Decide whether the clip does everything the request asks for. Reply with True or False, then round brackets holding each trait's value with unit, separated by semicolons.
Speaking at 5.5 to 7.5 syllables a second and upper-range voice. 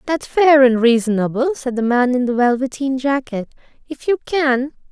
False (4.8 syllables/s; 260 Hz)